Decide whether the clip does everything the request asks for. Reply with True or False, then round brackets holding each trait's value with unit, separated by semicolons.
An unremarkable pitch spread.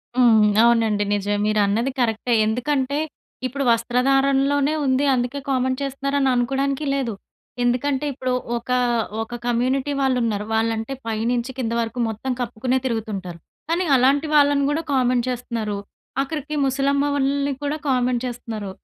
True (3.2 semitones)